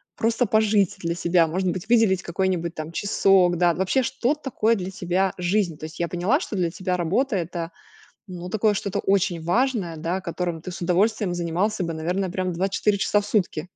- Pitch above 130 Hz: Yes, medium, 185 Hz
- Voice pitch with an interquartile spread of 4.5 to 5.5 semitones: No, average, 3.2 semitones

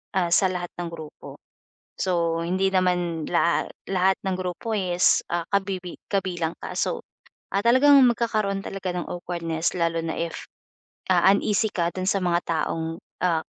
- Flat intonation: Yes, narrow, 2.3 semitones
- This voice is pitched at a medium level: Yes, medium, 180 Hz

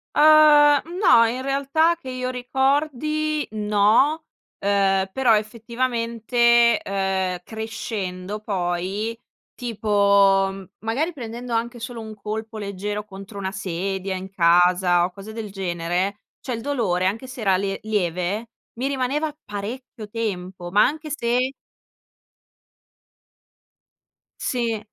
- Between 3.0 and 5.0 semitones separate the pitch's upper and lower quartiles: Yes, average, 4.6 semitones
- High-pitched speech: Yes, high, 220 Hz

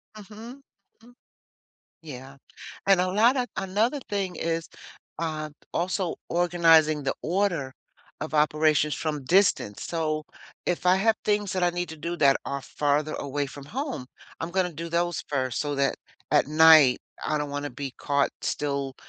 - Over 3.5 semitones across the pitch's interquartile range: Yes, average, 4.3 semitones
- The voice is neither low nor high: Yes, medium, 160 Hz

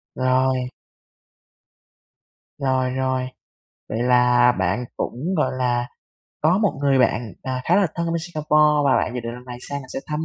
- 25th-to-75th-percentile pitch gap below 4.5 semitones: Yes, average, 3.4 semitones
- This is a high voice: No, low, 130 Hz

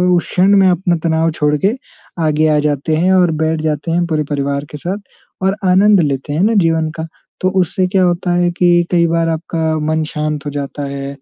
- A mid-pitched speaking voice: Yes, medium, 160 Hz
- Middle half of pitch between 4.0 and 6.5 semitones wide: No, average, 2.9 semitones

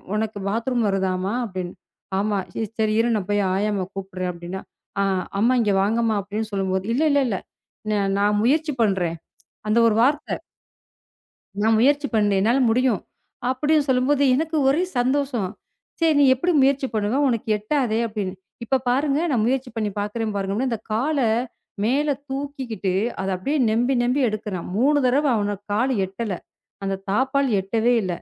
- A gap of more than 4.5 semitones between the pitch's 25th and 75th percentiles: Yes, average, 4.9 semitones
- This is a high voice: Yes, high, 225 Hz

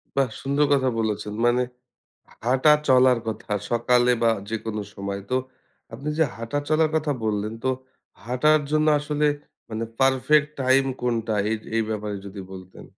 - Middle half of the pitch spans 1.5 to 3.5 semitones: No, average, 4.6 semitones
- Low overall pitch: Yes, low, 125 Hz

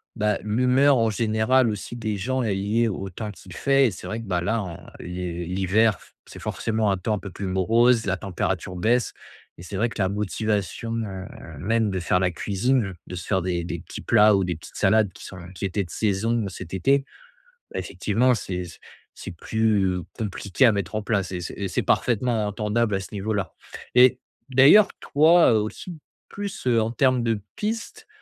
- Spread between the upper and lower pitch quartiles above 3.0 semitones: Yes, average, 3.7 semitones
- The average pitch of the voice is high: No, low, 105 Hz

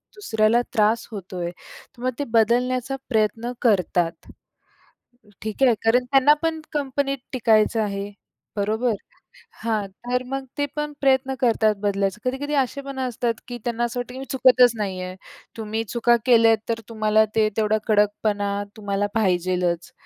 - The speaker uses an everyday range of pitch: Yes, average, 3.4 semitones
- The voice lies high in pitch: Yes, high, 225 Hz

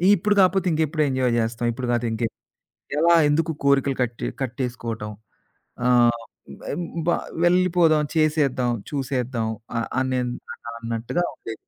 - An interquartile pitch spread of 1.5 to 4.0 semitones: No, average, 4.8 semitones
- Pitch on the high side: No, low, 130 Hz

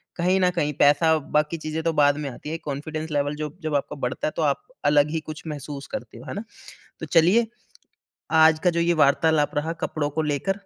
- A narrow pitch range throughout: Yes, narrow, 2.1 semitones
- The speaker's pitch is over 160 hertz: No, medium, 155 Hz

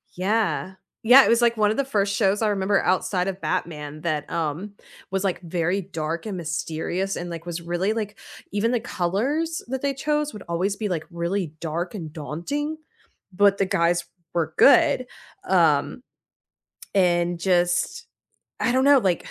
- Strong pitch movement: No, average, 4.2 semitones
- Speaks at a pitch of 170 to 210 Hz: Yes, high, 190 Hz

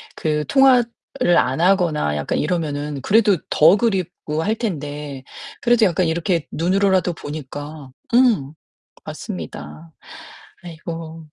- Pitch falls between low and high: Yes, medium, 165 Hz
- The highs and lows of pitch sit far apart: No, average, 4.9 semitones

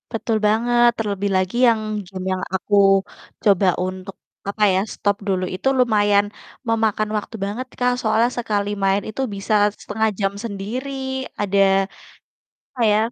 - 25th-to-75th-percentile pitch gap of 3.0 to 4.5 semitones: No, narrow, 2.4 semitones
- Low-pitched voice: No, high, 210 Hz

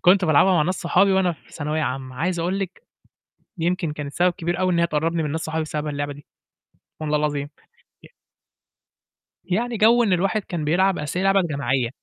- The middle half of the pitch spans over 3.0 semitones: Yes, average, 3.7 semitones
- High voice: No, medium, 170 Hz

